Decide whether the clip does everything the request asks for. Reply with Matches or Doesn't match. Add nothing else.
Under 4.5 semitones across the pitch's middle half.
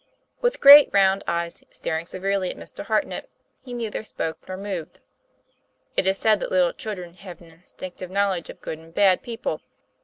Matches